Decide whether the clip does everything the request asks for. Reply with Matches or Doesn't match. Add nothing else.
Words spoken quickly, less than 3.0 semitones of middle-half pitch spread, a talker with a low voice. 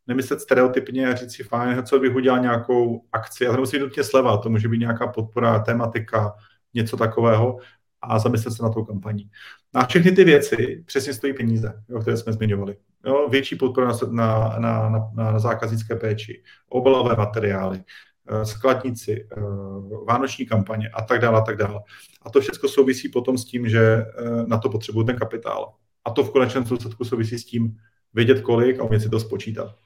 Matches